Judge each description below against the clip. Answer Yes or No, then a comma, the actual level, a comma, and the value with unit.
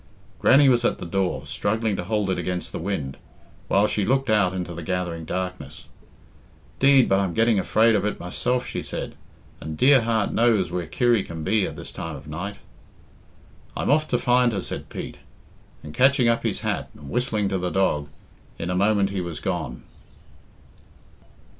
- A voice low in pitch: Yes, low, 100 Hz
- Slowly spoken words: No, average, 185 wpm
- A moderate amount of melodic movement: Yes, average, 4.7 semitones